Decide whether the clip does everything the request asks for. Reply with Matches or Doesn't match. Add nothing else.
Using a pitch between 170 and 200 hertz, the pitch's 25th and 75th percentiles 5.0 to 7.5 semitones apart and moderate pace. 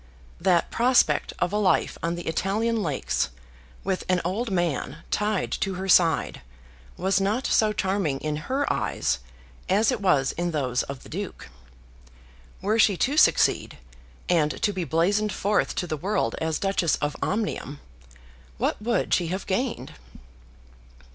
Doesn't match